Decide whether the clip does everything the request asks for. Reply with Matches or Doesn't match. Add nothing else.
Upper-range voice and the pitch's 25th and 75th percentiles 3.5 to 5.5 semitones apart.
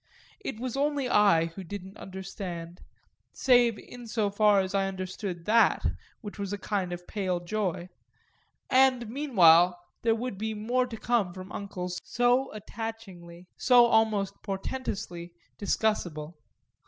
Matches